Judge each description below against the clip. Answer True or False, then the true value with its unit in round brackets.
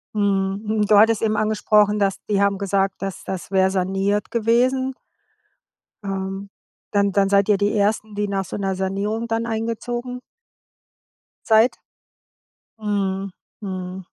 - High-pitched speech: True (205 Hz)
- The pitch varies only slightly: True (2.0 semitones)